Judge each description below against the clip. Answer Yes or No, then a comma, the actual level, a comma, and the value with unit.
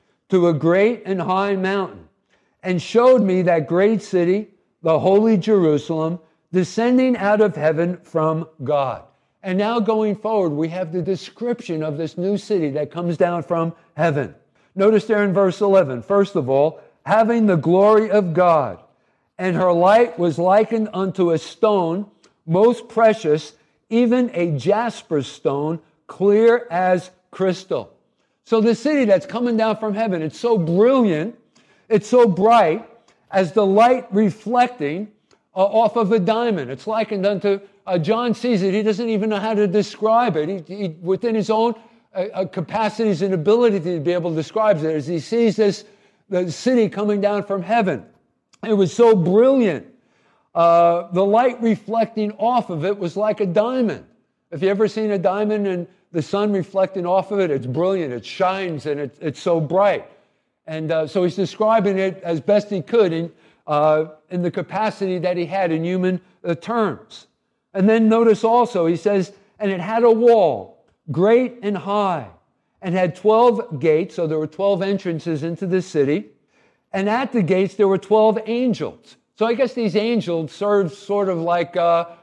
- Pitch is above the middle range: Yes, high, 195 Hz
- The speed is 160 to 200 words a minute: Yes, average, 170 wpm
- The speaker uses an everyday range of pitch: Yes, average, 4.1 semitones